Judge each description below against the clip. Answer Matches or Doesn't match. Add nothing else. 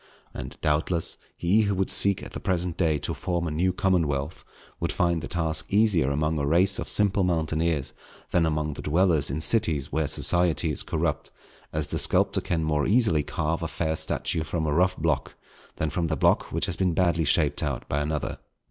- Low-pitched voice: Matches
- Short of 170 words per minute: Doesn't match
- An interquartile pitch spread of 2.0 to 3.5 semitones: Matches